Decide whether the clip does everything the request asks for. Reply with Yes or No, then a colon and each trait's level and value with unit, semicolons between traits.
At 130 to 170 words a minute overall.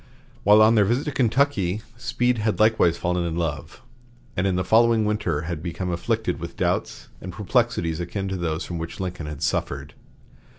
No: average, 180 wpm